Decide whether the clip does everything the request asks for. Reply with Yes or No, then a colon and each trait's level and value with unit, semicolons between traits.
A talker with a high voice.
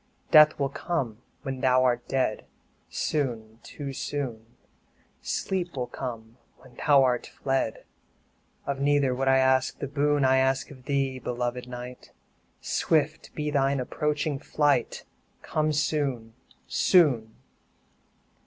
No: low, 135 Hz